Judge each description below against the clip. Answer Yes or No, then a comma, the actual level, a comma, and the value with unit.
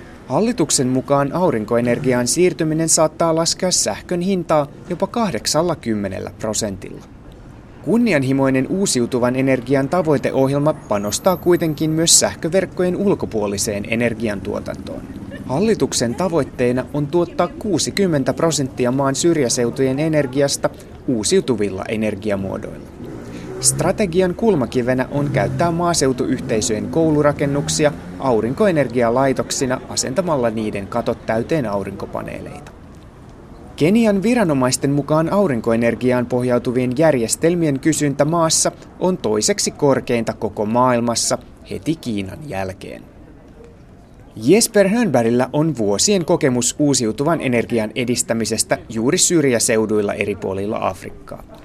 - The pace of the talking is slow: Yes, slow, 85 wpm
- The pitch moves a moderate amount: No, wide, 5.9 semitones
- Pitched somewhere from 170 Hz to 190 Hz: No, low, 135 Hz